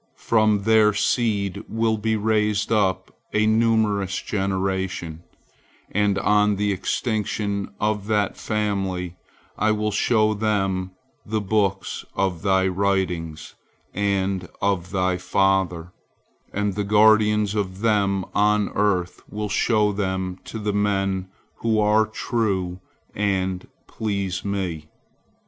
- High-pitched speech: No, low, 100 Hz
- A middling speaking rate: No, slow, 115 wpm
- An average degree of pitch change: No, narrow, 2.0 semitones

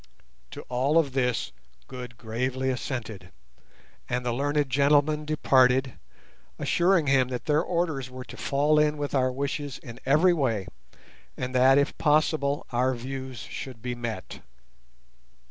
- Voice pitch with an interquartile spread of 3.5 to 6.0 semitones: No, average, 2.7 semitones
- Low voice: Yes, low, 130 Hz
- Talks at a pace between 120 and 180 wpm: Yes, average, 140 wpm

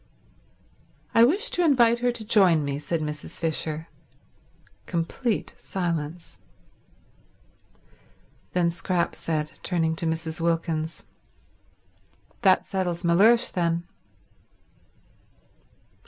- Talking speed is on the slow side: Yes, slow, 90 wpm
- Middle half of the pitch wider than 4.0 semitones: Yes, average, 4.4 semitones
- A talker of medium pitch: Yes, medium, 170 Hz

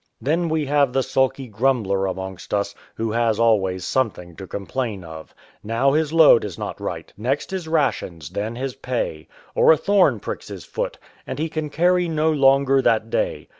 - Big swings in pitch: Yes, wide, 6.8 semitones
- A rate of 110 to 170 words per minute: No, average, 180 wpm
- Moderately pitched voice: No, low, 130 Hz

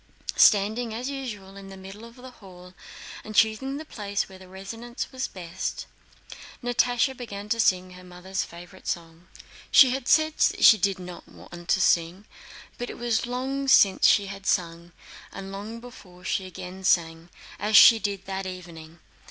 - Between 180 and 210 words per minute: No, average, 170 wpm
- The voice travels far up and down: No, average, 4.6 semitones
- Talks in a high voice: Yes, high, 195 Hz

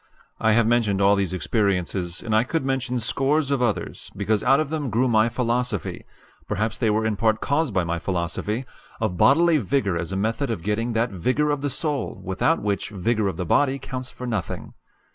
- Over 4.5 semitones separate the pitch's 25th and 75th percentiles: Yes, average, 4.9 semitones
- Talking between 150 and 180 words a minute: No, average, 200 wpm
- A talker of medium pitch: No, low, 115 Hz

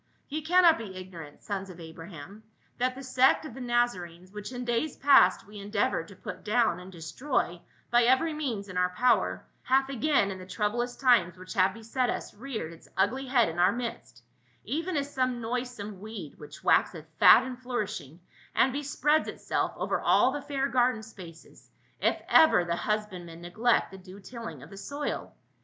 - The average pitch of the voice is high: Yes, high, 225 Hz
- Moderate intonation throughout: No, wide, 5.8 semitones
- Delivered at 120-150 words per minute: No, average, 185 wpm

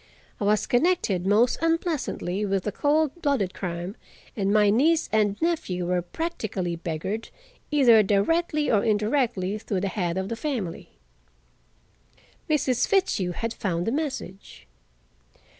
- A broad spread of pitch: Yes, wide, 7.4 semitones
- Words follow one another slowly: Yes, slow, 130 wpm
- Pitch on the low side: No, high, 215 Hz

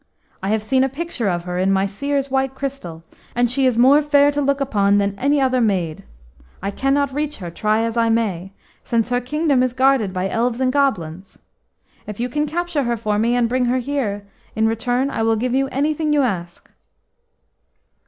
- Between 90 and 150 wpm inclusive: No, average, 200 wpm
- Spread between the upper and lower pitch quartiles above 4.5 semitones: Yes, average, 4.9 semitones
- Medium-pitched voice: No, high, 245 Hz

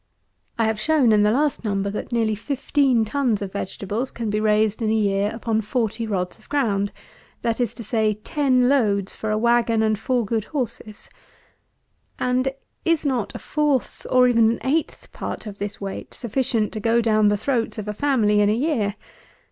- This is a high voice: Yes, high, 225 Hz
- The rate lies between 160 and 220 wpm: Yes, average, 190 wpm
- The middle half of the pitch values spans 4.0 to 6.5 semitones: No, average, 3.1 semitones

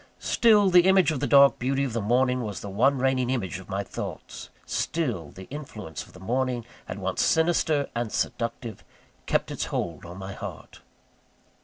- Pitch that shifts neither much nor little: No, wide, 5.8 semitones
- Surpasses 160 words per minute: Yes, average, 180 wpm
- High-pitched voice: No, low, 125 Hz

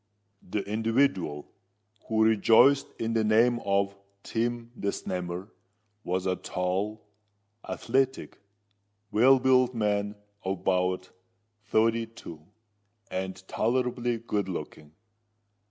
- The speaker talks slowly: Yes, slow, 100 wpm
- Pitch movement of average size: Yes, average, 3.9 semitones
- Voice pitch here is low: Yes, low, 110 Hz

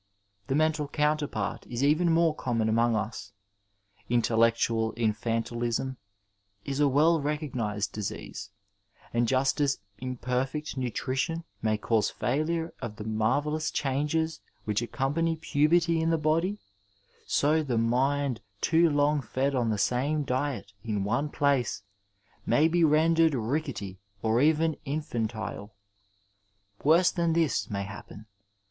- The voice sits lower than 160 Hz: Yes, low, 135 Hz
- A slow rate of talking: Yes, slow, 125 wpm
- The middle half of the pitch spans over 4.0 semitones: Yes, average, 5.1 semitones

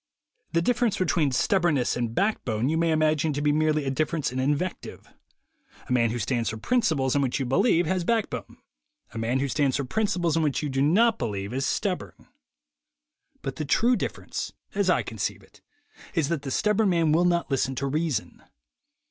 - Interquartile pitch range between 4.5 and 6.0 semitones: Yes, average, 4.9 semitones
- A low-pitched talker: No, medium, 150 Hz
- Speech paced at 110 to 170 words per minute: No, average, 190 wpm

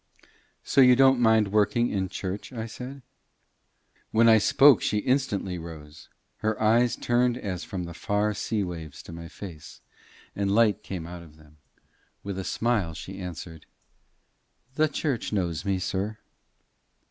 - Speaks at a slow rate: No, average, 150 wpm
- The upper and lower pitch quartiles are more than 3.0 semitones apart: Yes, average, 4.8 semitones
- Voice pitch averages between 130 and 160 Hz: No, low, 100 Hz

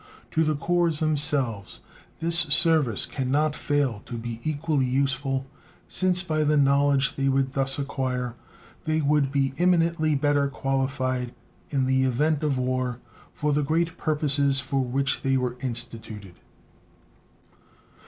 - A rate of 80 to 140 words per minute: Yes, slow, 135 wpm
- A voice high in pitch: No, medium, 140 Hz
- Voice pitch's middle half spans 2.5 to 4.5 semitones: Yes, average, 2.8 semitones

